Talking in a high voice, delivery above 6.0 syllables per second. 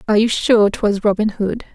No: high, 210 Hz; 5.4 syllables/s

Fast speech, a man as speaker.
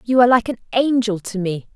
No: fast, 240 wpm; female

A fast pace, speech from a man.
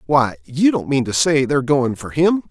Yes: fast, 240 wpm; male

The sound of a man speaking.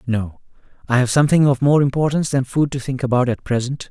Yes: male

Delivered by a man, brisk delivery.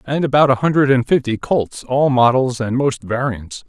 No: male; average, 195 wpm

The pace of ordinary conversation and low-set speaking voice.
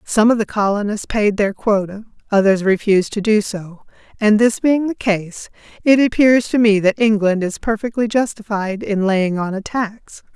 No: average, 180 wpm; high, 210 Hz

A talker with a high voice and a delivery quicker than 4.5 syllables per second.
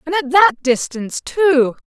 No: very high, 300 Hz; 4.2 syllables/s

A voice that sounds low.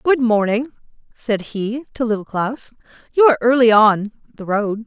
No: high, 230 Hz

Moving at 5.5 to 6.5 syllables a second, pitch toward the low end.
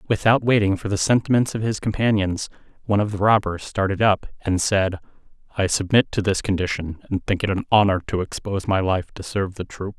Yes: 5.9 syllables/s; low, 100 Hz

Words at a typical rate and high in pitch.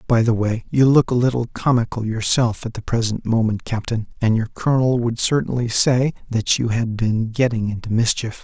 No: average, 190 wpm; low, 115 Hz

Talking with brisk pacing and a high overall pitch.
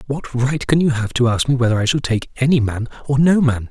No: fast, 275 wpm; low, 130 Hz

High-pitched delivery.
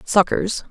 Yes: high, 205 Hz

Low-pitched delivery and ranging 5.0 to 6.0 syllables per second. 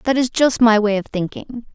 No: high, 230 Hz; 5.1 syllables/s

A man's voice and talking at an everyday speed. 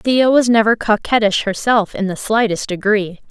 No: female; average, 165 wpm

